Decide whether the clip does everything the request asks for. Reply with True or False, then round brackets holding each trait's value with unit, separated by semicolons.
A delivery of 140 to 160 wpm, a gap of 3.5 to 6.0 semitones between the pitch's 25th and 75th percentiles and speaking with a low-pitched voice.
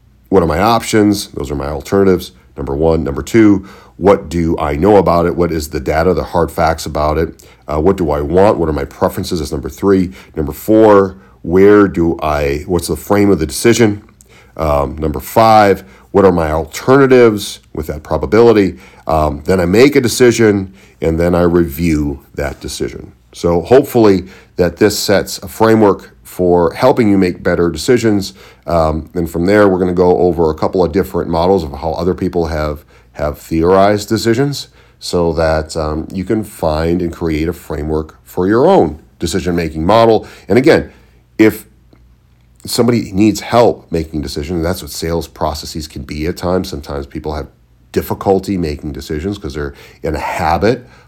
False (175 wpm; 4.3 semitones; 85 Hz)